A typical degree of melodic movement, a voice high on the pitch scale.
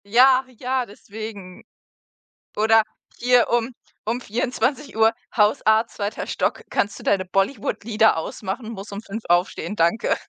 Yes: average, 3.1 semitones; high, 220 Hz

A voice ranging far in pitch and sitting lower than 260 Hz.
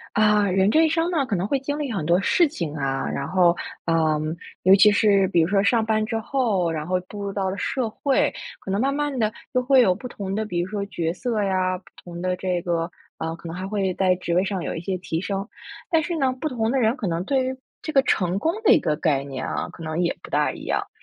Yes: wide, 5.7 semitones; high, 195 Hz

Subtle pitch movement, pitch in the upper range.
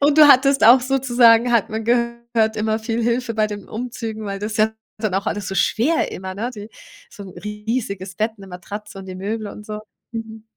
Yes: narrow, 2.2 semitones; high, 220 Hz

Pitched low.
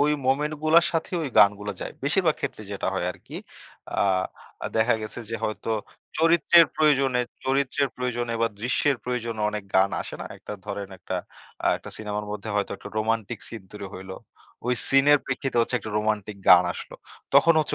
Yes: low, 120 Hz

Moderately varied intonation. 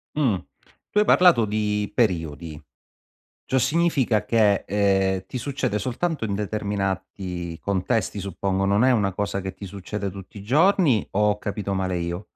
Yes: average, 3.4 semitones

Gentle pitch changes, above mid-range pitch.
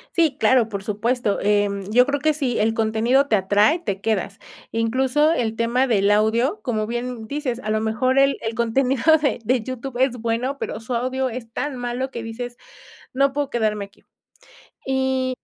No: average, 3.1 semitones; high, 240 Hz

